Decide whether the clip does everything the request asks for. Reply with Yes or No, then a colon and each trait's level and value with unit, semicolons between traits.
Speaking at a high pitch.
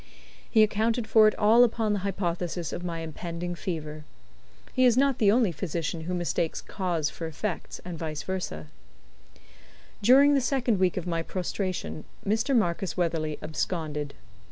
No: medium, 180 Hz